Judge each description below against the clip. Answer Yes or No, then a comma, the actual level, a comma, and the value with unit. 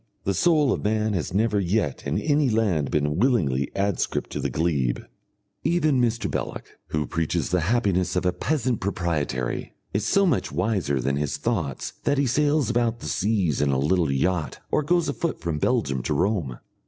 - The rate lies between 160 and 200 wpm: Yes, average, 180 wpm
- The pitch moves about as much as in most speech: No, wide, 8.2 semitones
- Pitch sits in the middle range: No, very low, 95 Hz